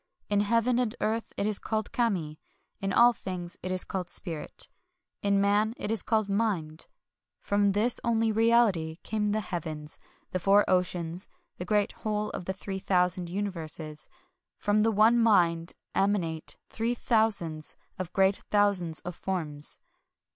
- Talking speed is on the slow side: No, average, 155 wpm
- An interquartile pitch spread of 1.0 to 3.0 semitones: No, average, 3.7 semitones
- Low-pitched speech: No, high, 200 Hz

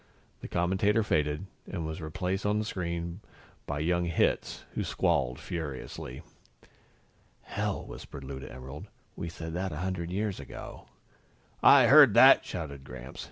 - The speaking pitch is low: Yes, very low, 85 Hz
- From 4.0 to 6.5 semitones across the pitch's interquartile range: Yes, average, 4.6 semitones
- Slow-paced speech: No, average, 145 wpm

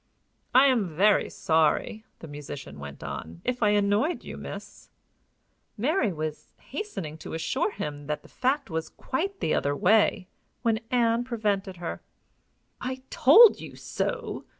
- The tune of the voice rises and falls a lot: Yes, wide, 8.4 semitones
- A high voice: Yes, high, 205 Hz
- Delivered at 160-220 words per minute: No, average, 145 wpm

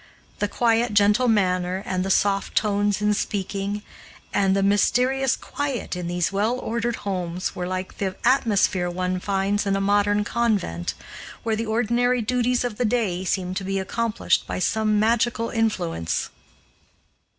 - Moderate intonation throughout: Yes, average, 3.4 semitones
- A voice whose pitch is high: Yes, high, 205 Hz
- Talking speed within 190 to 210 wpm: No, average, 150 wpm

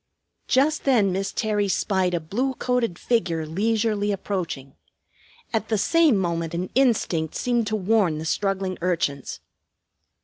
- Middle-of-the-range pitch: No, high, 200 Hz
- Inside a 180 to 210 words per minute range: No, slow, 135 wpm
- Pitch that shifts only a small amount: No, average, 4.7 semitones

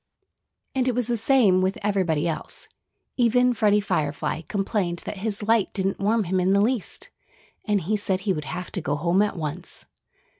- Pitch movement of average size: Yes, average, 3.5 semitones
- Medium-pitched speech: No, high, 195 Hz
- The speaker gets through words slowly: No, average, 185 wpm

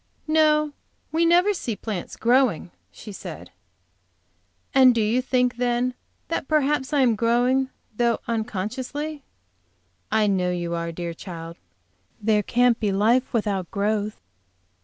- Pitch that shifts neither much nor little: Yes, average, 4.5 semitones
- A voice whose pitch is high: Yes, high, 235 Hz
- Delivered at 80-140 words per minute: Yes, slow, 135 wpm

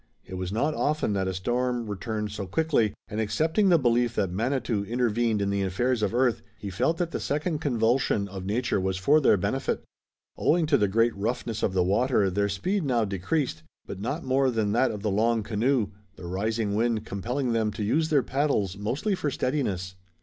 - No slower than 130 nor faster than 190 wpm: No, average, 200 wpm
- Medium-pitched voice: No, low, 115 Hz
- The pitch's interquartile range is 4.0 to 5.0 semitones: Yes, average, 4.7 semitones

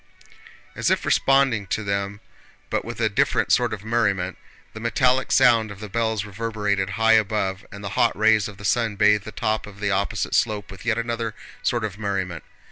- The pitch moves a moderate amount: No, narrow, 2.1 semitones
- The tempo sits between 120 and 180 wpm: No, average, 195 wpm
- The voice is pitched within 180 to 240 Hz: No, low, 105 Hz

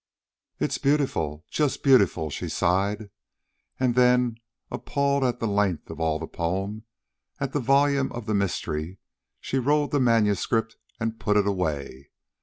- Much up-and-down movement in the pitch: Yes, wide, 6.2 semitones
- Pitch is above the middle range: No, low, 110 Hz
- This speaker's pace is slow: No, average, 145 wpm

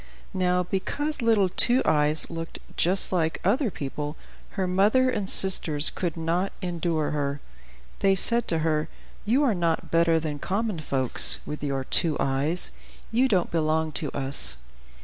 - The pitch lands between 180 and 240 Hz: No, medium, 170 Hz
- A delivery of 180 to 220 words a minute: No, average, 150 wpm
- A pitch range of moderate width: Yes, average, 4.2 semitones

